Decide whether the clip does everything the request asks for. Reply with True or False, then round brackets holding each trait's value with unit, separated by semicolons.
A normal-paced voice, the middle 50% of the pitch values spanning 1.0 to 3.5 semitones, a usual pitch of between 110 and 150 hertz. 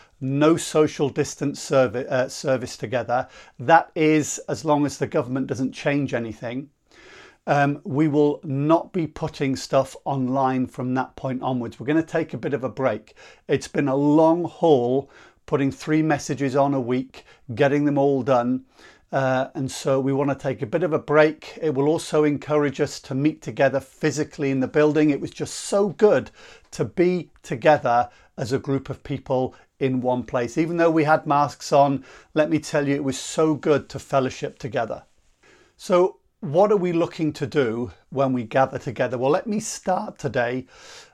True (185 wpm; 2.7 semitones; 140 Hz)